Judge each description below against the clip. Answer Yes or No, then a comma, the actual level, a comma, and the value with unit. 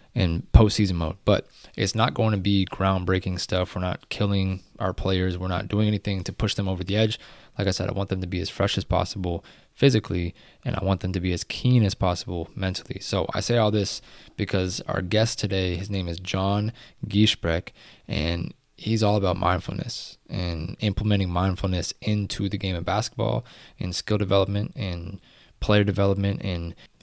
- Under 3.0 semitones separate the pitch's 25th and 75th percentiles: Yes, narrow, 2.4 semitones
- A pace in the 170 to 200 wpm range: Yes, average, 185 wpm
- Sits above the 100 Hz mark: No, very low, 95 Hz